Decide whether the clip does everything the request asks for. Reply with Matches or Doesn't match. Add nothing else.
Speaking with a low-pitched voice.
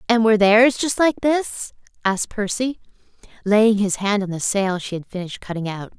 Doesn't match